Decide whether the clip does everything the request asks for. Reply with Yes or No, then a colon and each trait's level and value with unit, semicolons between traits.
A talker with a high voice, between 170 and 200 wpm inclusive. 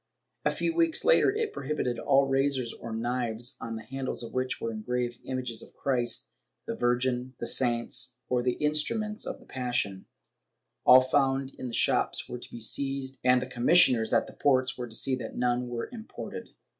No: low, 125 Hz; average, 190 wpm